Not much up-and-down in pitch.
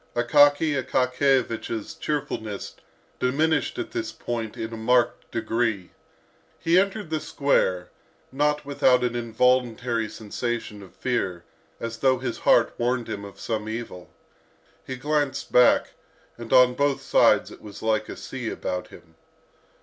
No: average, 3.6 semitones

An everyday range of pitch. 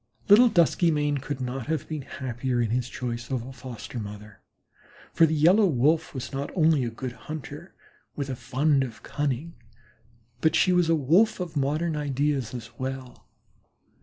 Yes: average, 4.1 semitones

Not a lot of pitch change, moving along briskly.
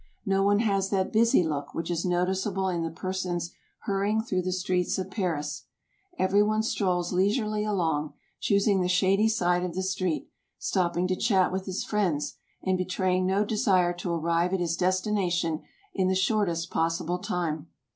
No: narrow, 2.2 semitones; average, 165 wpm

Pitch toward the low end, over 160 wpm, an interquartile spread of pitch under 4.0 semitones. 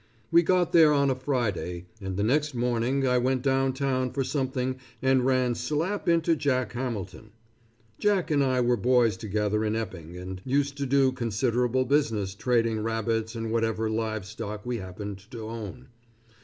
Yes: low, 125 Hz; average, 170 wpm; average, 3.5 semitones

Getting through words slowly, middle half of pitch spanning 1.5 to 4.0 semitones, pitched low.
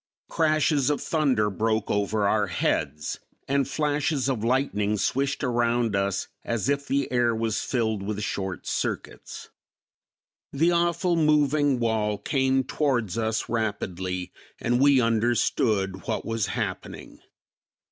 No: slow, 125 wpm; average, 4.9 semitones; low, 120 Hz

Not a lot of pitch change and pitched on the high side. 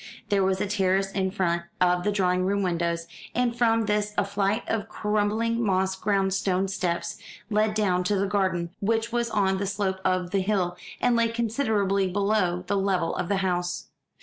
Yes: narrow, 2.3 semitones; high, 195 Hz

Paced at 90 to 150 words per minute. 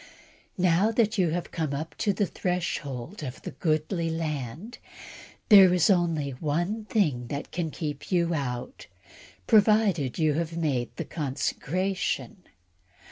Yes: slow, 135 wpm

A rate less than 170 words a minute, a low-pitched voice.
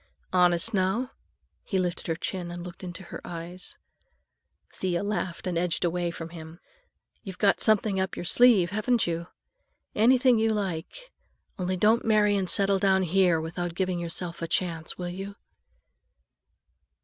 No: average, 150 wpm; medium, 185 Hz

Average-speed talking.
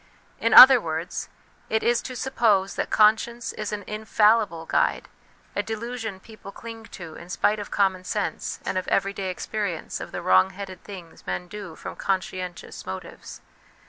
Yes: average, 160 wpm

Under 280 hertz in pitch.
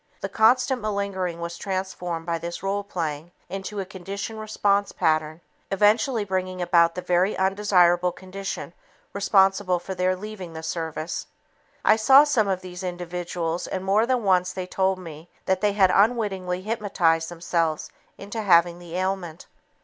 Yes: medium, 185 Hz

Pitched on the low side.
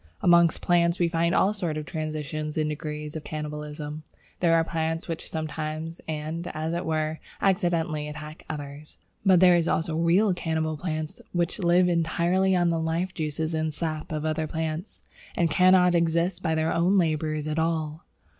No: medium, 160 Hz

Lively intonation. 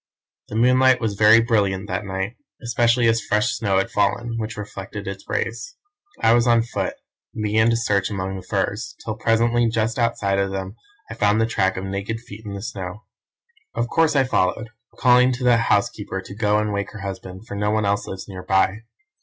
No: average, 3.0 semitones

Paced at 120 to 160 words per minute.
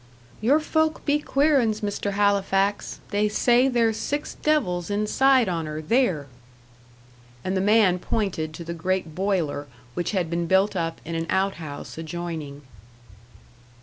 Yes: average, 150 wpm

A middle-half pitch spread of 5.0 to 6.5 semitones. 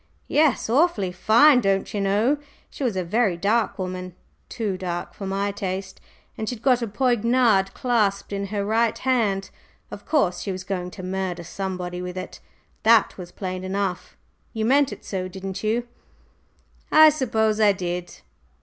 No: average, 3.8 semitones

